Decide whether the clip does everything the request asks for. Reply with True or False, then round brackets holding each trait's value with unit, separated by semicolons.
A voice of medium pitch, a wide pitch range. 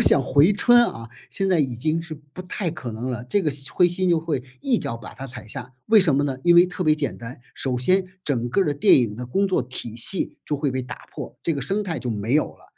True (145 Hz; 6.1 semitones)